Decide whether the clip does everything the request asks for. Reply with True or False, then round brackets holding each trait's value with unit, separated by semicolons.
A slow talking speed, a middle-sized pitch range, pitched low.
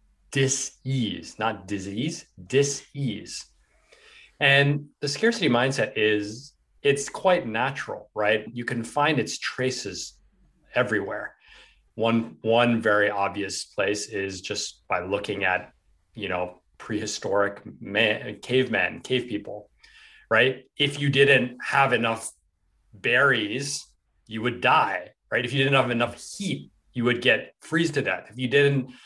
True (130 wpm; 4.9 semitones; 120 Hz)